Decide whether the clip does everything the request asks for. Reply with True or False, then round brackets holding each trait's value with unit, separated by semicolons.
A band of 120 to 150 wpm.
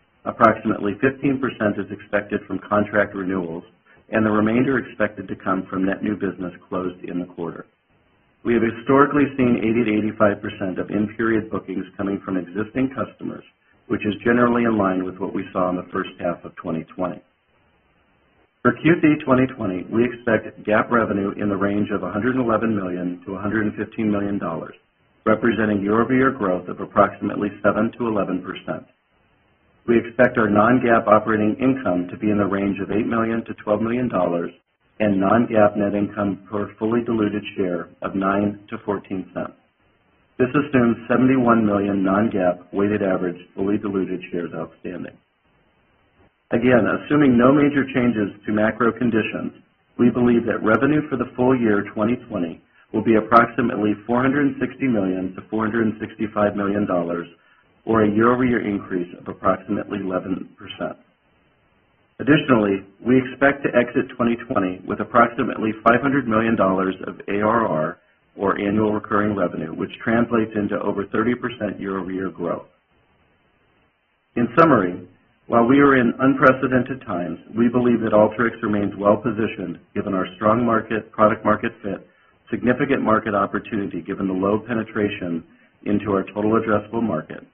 True (145 wpm)